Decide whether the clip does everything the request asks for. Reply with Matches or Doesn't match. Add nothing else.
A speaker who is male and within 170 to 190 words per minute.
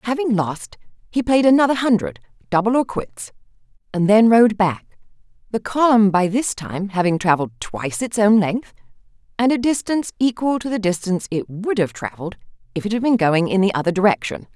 Doesn't match